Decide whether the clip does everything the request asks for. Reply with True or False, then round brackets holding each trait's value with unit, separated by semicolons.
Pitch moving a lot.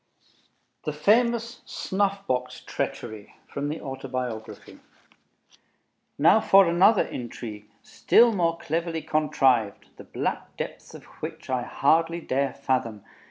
True (6.5 semitones)